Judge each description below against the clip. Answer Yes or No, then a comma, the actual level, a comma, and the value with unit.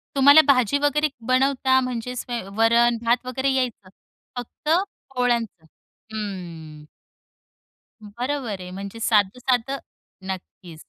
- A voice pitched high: Yes, high, 240 Hz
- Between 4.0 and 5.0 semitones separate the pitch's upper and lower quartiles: Yes, average, 4.3 semitones